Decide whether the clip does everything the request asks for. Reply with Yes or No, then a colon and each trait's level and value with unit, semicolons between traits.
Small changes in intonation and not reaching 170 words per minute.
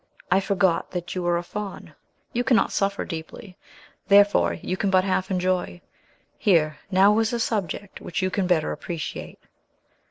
Yes: narrow, 2.2 semitones; average, 160 wpm